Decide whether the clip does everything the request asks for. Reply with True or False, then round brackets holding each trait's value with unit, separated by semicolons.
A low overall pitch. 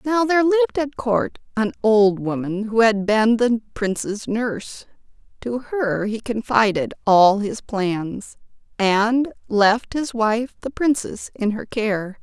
False (225 Hz)